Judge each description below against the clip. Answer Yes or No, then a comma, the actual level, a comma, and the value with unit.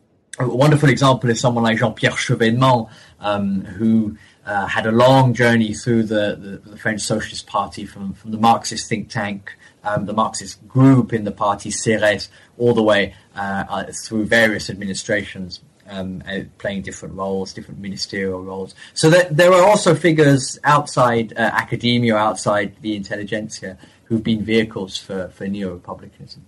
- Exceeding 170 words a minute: No, average, 160 wpm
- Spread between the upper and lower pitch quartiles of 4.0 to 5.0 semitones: No, average, 3.1 semitones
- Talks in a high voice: No, low, 110 Hz